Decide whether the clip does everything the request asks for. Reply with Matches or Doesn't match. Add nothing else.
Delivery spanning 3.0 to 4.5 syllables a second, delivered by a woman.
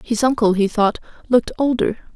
Doesn't match